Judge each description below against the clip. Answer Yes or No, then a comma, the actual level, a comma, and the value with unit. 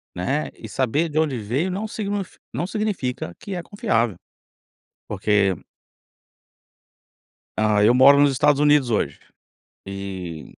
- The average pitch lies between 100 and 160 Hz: Yes, low, 135 Hz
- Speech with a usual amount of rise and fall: No, wide, 8.0 semitones